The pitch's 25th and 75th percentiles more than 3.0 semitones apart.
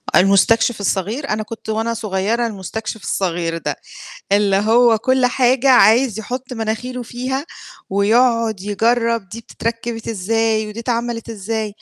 No: narrow, 2.6 semitones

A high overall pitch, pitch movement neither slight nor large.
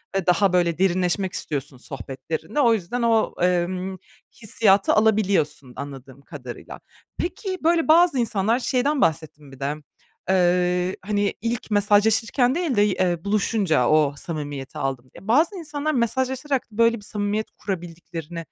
No: high, 195 Hz; wide, 6.0 semitones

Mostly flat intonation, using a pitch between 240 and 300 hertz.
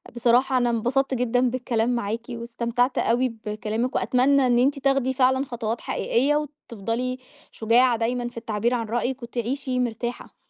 Yes: narrow, 1.8 semitones; high, 245 Hz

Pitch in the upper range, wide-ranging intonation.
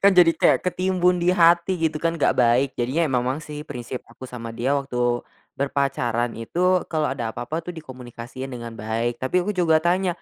No: low, 135 Hz; wide, 5.9 semitones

